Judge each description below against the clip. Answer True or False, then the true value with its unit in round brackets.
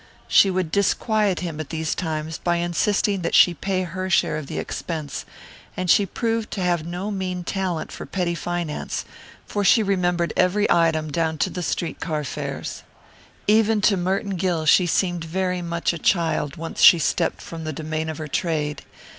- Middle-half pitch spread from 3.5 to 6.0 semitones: False (2.9 semitones)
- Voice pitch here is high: False (175 Hz)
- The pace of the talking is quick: False (180 wpm)